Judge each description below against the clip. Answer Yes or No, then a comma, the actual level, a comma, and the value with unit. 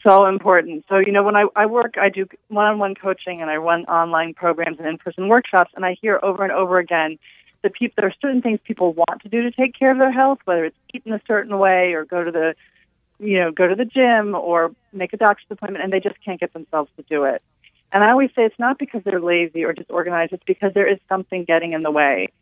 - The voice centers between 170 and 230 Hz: Yes, high, 190 Hz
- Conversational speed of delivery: No, fast, 255 wpm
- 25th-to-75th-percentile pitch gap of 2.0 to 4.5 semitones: Yes, average, 3.8 semitones